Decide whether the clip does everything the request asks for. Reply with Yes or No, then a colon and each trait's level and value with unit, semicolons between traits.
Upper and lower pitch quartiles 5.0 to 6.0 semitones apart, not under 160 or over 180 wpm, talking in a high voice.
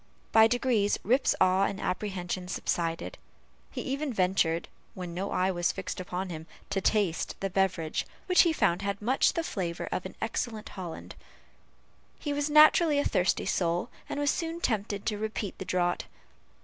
Yes: average, 5.3 semitones; average, 165 wpm; high, 195 Hz